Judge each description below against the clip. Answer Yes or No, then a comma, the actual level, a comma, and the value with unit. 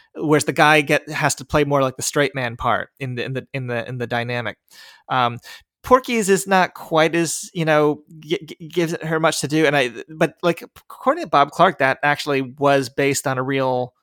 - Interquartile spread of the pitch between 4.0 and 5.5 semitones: No, average, 3.5 semitones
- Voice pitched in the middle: Yes, medium, 145 Hz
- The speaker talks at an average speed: No, fast, 225 wpm